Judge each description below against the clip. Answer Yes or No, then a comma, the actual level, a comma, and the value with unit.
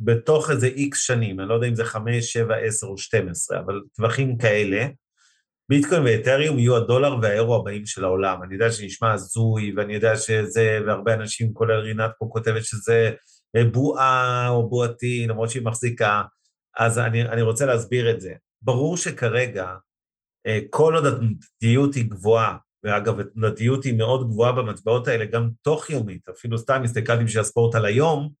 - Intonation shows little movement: Yes, narrow, 2.3 semitones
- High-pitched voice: No, low, 115 Hz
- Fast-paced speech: Yes, fast, 165 wpm